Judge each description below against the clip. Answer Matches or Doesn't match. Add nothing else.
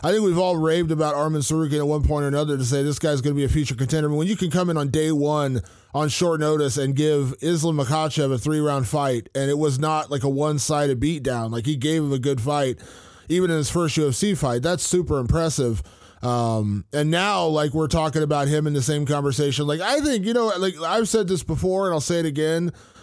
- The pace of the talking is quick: Matches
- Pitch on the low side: Doesn't match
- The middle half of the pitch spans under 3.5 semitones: Matches